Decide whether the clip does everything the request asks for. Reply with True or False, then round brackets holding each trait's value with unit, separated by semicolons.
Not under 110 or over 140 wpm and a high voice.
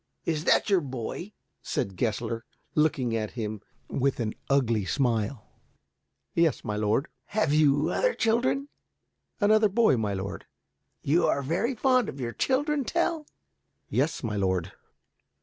False (135 wpm; 140 Hz)